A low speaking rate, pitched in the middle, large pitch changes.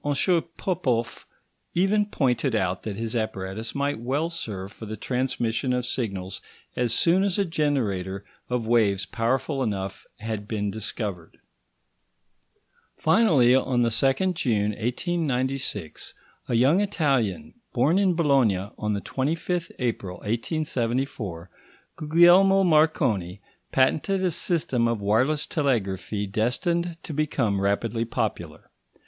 No: slow, 120 wpm; low, 125 Hz; wide, 6.4 semitones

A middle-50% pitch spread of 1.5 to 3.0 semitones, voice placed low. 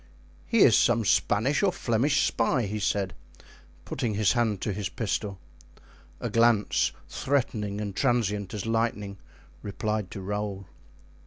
Yes: narrow, 2.6 semitones; low, 105 Hz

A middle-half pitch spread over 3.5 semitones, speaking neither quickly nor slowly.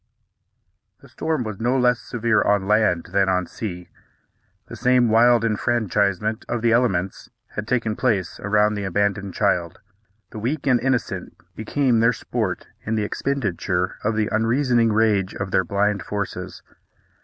No: average, 3.2 semitones; average, 150 wpm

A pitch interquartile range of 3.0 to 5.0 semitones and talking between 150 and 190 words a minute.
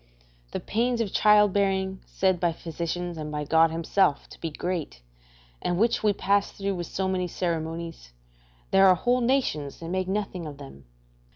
Yes: average, 3.4 semitones; average, 175 wpm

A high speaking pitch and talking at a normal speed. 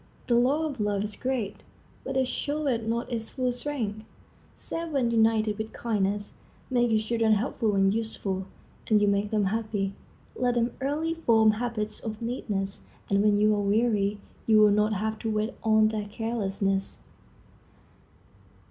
Yes: high, 220 Hz; average, 160 wpm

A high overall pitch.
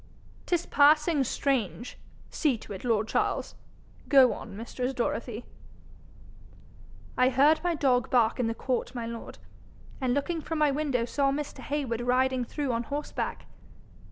Yes: very high, 260 Hz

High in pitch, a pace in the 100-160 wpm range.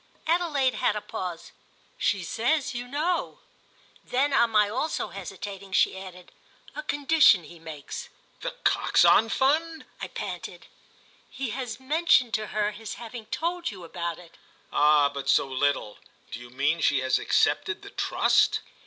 Yes: high, 215 Hz; average, 150 wpm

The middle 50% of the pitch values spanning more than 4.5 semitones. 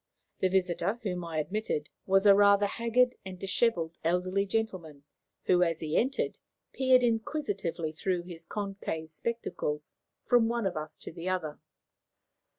Yes: average, 4.9 semitones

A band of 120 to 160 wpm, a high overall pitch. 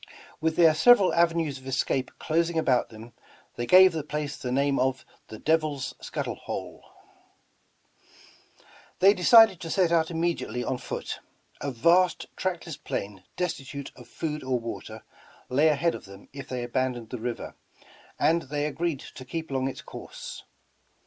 No: average, 155 wpm; medium, 145 Hz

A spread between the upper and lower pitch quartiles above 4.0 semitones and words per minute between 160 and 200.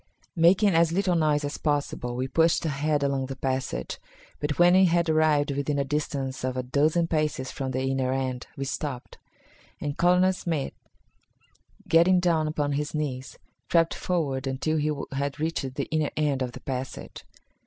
No: average, 3.4 semitones; average, 170 wpm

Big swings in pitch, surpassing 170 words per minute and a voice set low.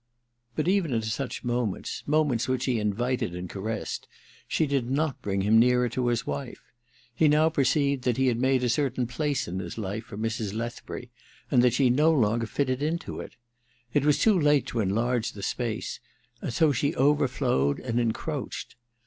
No: average, 3.9 semitones; average, 190 wpm; low, 125 Hz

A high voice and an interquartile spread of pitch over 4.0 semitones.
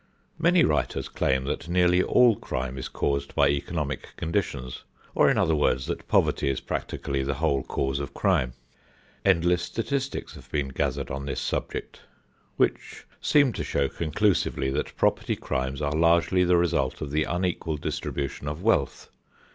No: very low, 75 Hz; average, 4.5 semitones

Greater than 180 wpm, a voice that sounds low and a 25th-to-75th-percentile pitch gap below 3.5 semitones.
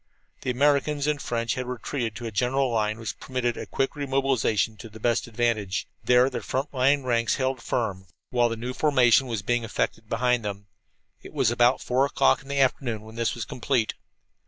Yes: average, 200 wpm; low, 120 Hz; average, 2.7 semitones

